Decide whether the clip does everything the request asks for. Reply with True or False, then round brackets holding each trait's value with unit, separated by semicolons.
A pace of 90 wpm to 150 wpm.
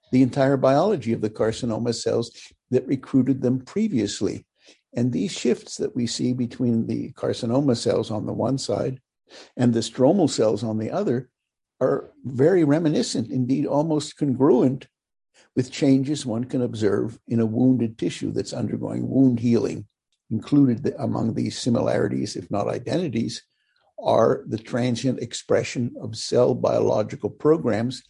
True (140 wpm)